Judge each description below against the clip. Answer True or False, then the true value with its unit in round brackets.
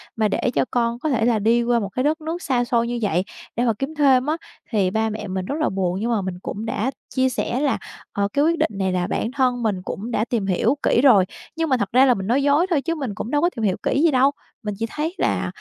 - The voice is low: False (240 Hz)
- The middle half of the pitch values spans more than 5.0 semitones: False (4.7 semitones)